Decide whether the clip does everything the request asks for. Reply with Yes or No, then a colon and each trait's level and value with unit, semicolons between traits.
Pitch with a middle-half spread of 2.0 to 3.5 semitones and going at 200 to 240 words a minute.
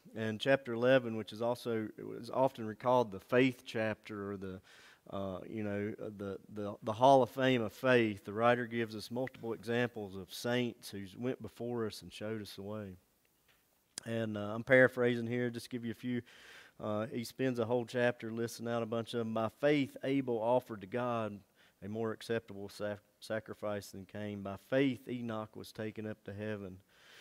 No: average, 2.8 semitones; average, 185 wpm